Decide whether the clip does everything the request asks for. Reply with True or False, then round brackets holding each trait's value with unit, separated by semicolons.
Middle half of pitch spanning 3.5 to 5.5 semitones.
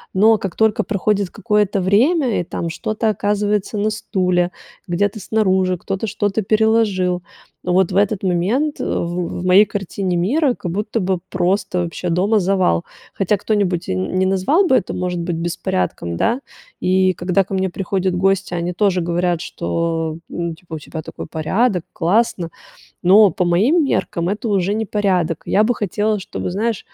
False (3.0 semitones)